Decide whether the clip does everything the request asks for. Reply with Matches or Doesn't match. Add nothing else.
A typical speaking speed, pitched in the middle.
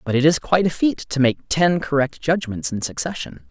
Doesn't match